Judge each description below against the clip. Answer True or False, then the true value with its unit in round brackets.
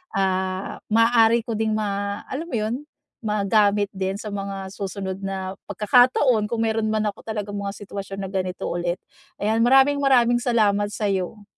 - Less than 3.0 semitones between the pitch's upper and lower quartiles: True (2.5 semitones)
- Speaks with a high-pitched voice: True (205 Hz)